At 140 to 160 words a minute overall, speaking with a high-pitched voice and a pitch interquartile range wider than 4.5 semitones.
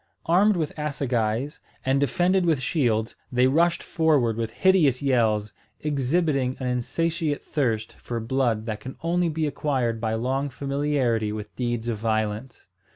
No: average, 145 wpm; low, 130 Hz; average, 4.9 semitones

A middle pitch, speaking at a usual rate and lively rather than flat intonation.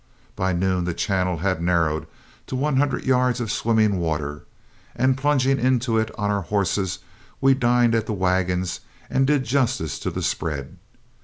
No: low, 105 Hz; average, 165 wpm; wide, 6.0 semitones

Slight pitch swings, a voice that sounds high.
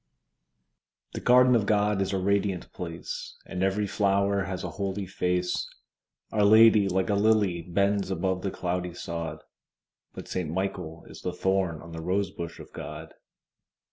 No: narrow, 2.3 semitones; very low, 95 Hz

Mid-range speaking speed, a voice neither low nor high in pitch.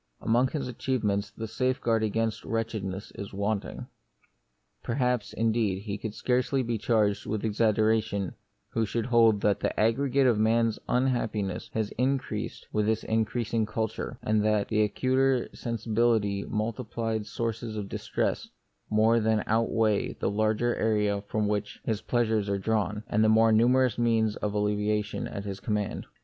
No: average, 155 wpm; low, 110 Hz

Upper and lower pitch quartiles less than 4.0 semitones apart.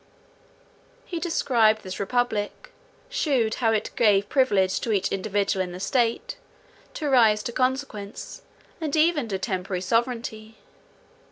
No: average, 4.5 semitones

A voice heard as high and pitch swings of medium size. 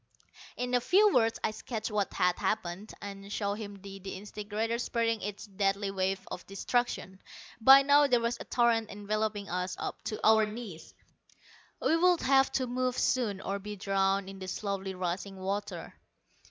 Yes: high, 210 Hz; average, 3.2 semitones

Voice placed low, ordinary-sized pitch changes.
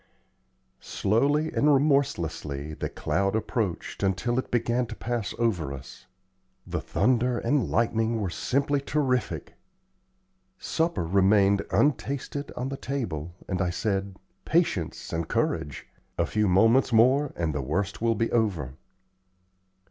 No: low, 110 Hz; wide, 5.8 semitones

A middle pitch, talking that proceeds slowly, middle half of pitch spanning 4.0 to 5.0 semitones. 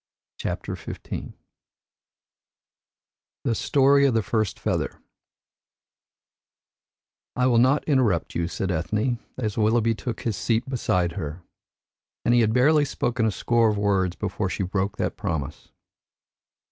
No: low, 110 Hz; slow, 130 wpm; average, 4.7 semitones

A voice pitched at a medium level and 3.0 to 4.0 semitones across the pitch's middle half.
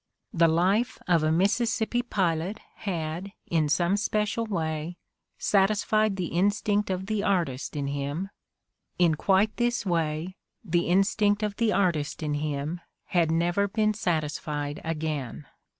No: medium, 180 Hz; average, 4.5 semitones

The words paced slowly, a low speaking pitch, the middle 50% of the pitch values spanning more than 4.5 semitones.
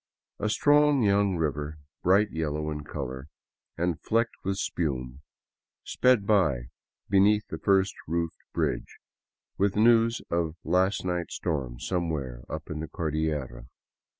Yes: slow, 125 wpm; very low, 85 Hz; average, 5.0 semitones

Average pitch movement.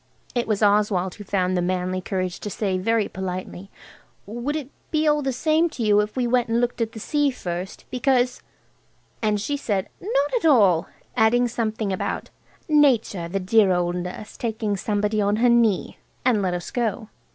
Yes: average, 4.4 semitones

